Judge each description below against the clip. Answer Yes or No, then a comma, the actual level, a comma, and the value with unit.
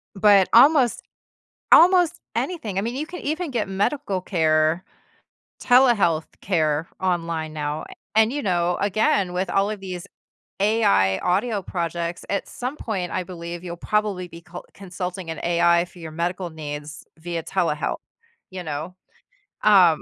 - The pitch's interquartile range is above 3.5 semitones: Yes, average, 3.9 semitones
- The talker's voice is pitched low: No, medium, 180 Hz